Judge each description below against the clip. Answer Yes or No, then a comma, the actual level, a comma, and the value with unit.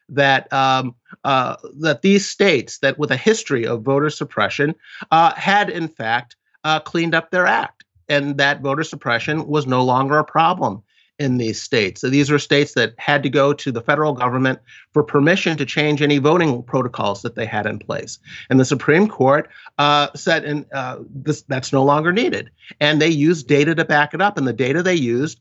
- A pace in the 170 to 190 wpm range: No, average, 200 wpm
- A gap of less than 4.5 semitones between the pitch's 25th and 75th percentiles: Yes, average, 2.7 semitones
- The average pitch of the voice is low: No, medium, 145 Hz